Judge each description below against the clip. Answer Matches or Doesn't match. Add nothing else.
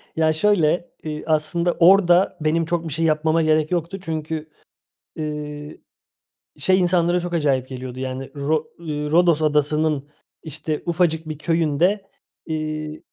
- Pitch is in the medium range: Matches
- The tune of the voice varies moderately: Doesn't match